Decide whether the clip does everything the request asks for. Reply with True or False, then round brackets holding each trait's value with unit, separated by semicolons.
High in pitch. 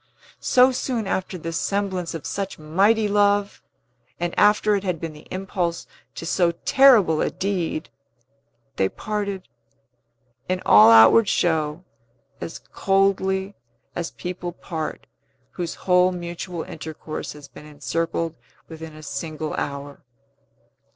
False (175 Hz)